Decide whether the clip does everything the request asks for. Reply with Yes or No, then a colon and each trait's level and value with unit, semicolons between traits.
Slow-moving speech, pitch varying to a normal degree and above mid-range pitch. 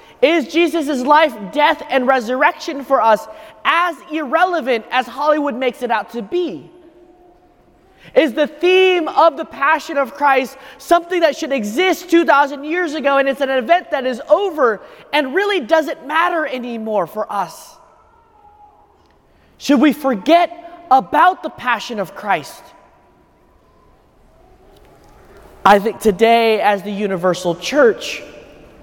Yes: slow, 125 wpm; average, 5.0 semitones; very high, 300 Hz